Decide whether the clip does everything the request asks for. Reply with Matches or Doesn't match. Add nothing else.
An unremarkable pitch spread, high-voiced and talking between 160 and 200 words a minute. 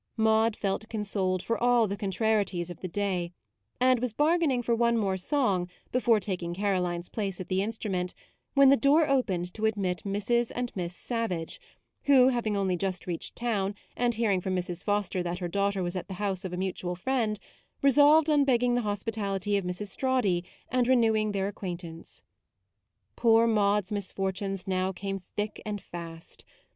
Matches